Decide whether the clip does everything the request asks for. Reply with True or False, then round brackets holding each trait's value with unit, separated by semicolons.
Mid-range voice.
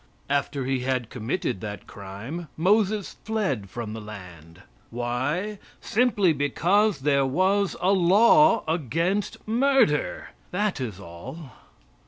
True (155 Hz)